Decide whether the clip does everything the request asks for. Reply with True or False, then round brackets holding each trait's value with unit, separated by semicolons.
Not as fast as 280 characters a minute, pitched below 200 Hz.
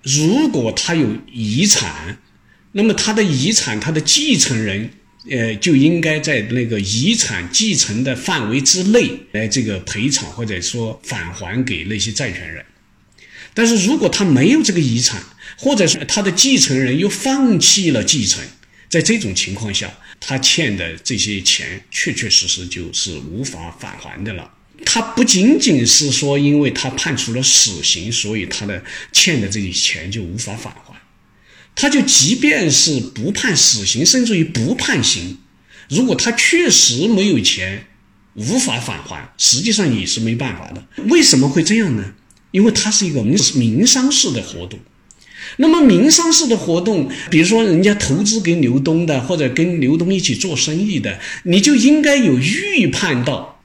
True (245 characters per minute; 140 Hz)